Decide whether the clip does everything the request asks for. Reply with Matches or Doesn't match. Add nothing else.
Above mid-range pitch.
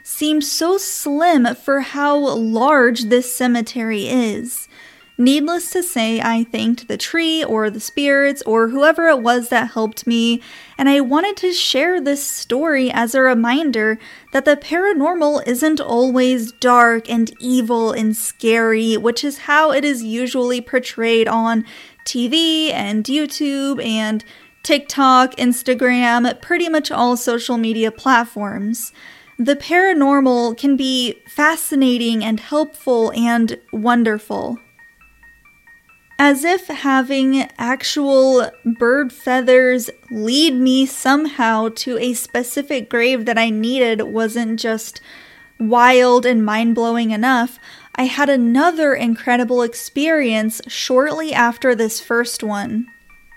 Matches